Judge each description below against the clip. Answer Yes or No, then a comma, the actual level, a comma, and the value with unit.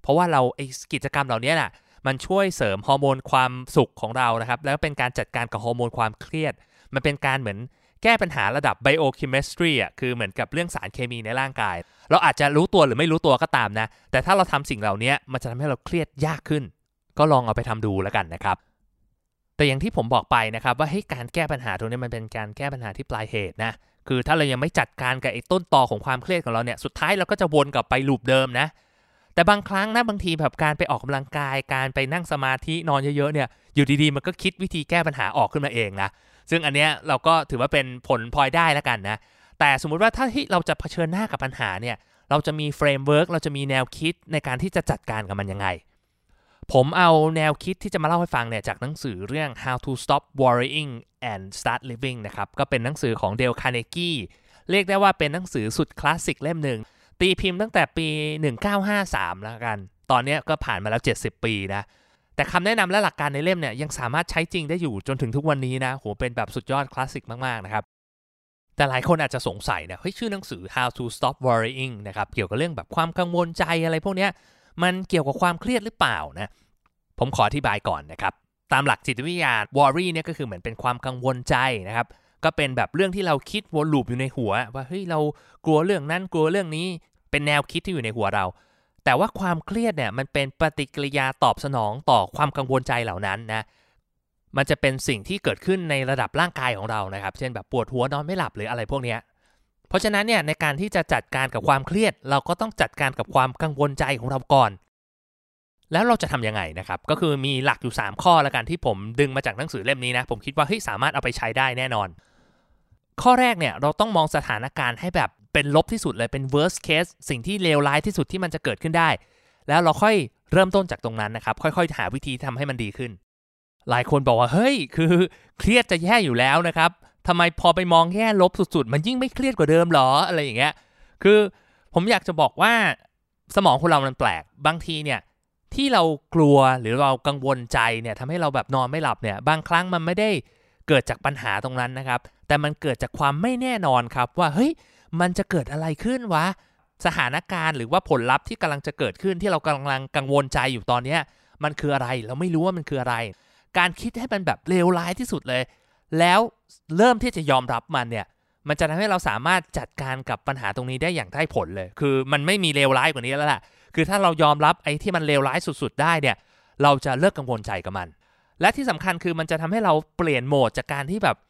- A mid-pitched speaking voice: Yes, medium, 145 Hz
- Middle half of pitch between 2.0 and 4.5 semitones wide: No, average, 5.0 semitones